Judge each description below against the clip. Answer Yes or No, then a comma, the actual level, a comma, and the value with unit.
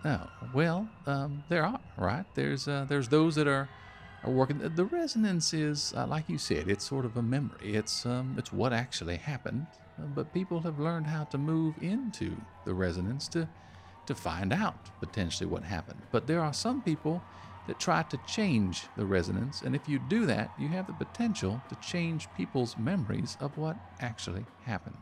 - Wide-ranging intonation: Yes, wide, 7.7 semitones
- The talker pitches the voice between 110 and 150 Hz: Yes, low, 135 Hz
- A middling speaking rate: Yes, average, 185 wpm